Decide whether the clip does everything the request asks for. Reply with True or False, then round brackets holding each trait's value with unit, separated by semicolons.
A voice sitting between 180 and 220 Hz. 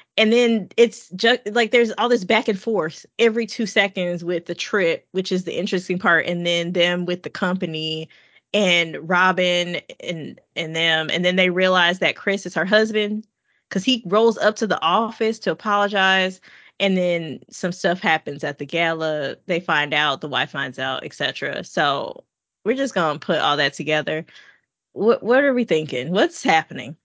True (185 Hz)